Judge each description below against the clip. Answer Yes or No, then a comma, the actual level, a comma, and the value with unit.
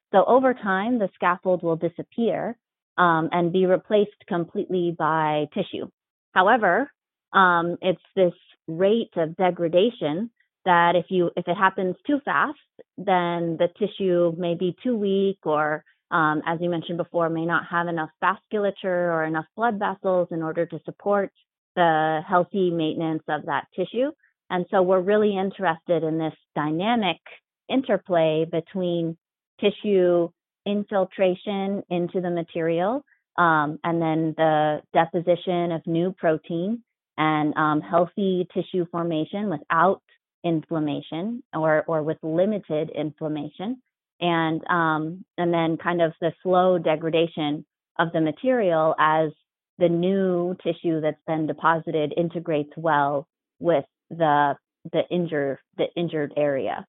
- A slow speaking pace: Yes, slow, 130 wpm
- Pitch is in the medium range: Yes, medium, 170 Hz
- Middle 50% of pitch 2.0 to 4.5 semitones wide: Yes, average, 2.9 semitones